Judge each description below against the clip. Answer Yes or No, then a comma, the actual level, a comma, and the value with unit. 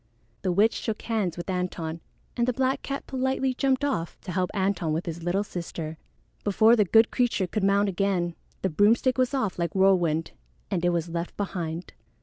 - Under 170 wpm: No, average, 185 wpm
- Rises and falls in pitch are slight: No, average, 4.7 semitones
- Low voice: No, high, 195 Hz